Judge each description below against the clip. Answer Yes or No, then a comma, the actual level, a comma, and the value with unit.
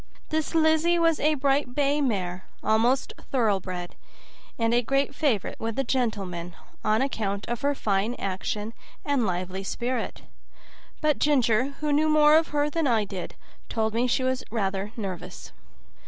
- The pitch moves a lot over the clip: Yes, wide, 6.0 semitones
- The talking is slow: No, average, 155 wpm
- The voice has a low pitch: No, high, 240 Hz